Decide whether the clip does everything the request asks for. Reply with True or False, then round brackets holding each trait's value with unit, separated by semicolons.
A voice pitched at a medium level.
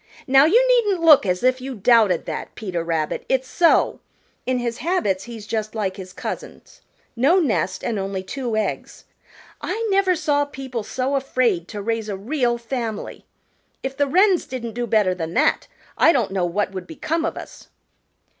False (240 Hz)